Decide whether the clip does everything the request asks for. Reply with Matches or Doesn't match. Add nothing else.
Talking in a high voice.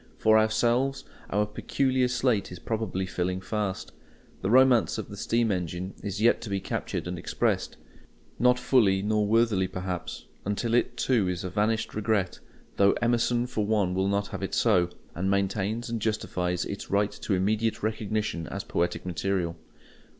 Doesn't match